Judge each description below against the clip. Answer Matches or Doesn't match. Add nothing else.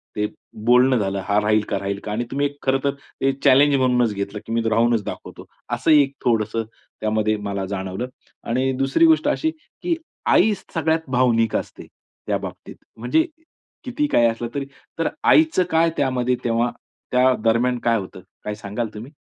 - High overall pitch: Doesn't match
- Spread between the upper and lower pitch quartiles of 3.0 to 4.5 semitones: Matches